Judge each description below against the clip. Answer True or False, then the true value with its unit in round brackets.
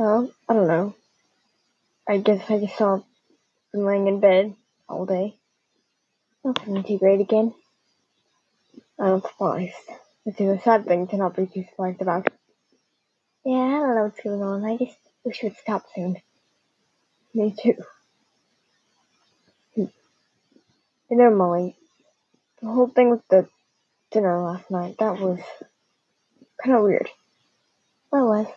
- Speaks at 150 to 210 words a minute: False (135 wpm)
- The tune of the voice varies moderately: True (3.4 semitones)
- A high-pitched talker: True (205 Hz)